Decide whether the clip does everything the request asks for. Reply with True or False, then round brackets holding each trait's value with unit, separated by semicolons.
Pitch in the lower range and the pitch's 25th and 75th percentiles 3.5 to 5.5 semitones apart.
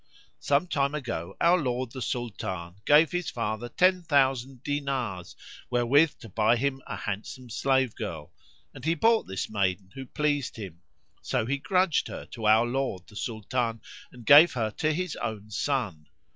True (125 Hz; 4.9 semitones)